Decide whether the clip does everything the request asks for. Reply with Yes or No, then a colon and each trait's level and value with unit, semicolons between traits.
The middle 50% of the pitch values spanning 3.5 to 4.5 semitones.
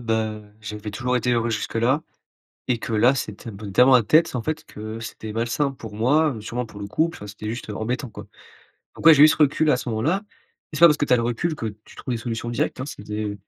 Yes: average, 4.0 semitones